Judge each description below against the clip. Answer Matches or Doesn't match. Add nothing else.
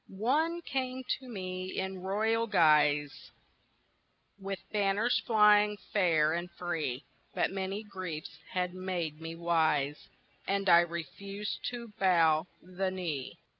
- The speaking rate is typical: Doesn't match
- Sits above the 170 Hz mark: Matches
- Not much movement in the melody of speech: Doesn't match